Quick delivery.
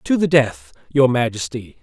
No: average, 165 wpm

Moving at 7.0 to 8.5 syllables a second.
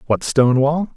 No: 5.1 syllables/s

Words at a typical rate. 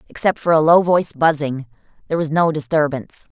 Yes: average, 175 wpm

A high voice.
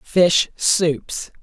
No: medium, 170 Hz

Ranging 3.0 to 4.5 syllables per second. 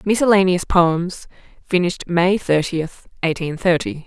Yes: 4.3 syllables/s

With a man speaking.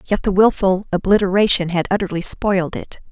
No: female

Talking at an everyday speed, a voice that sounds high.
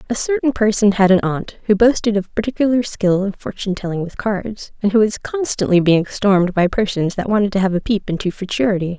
No: fast, 215 wpm; high, 205 Hz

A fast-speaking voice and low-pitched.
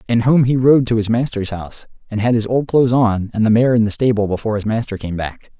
Yes: fast, 270 wpm; low, 115 Hz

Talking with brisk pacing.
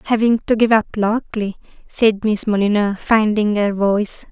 No: average, 155 wpm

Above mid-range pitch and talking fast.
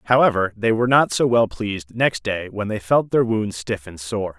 No: low, 110 Hz; fast, 235 wpm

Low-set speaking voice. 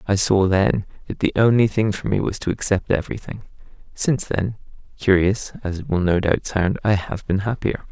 Yes: low, 100 Hz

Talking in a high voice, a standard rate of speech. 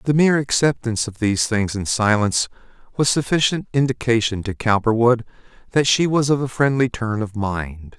No: low, 120 Hz; average, 165 wpm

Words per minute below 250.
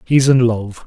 Yes: fast, 210 wpm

